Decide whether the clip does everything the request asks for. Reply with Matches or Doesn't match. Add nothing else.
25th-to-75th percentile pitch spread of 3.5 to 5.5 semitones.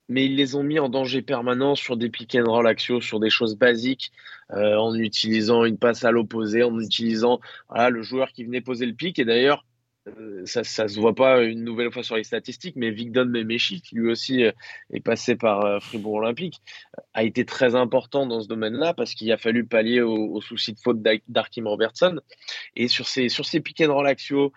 Doesn't match